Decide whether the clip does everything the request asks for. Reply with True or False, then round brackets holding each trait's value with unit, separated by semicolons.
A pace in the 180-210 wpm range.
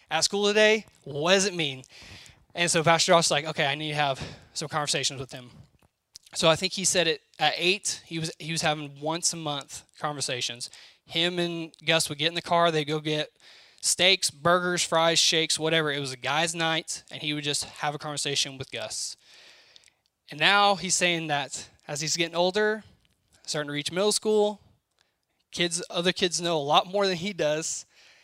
True (200 wpm)